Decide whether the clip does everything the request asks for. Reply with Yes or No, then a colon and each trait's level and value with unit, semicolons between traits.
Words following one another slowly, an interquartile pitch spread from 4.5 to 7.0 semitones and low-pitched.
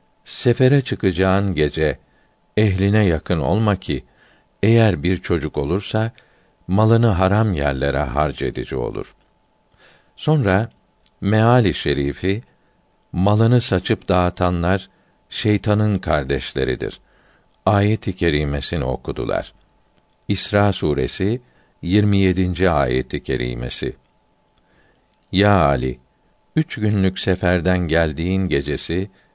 Yes: slow, 80 wpm; wide, 5.5 semitones; very low, 95 Hz